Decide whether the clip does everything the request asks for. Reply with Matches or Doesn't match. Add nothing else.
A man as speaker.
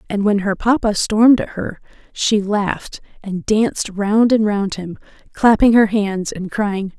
Doesn't match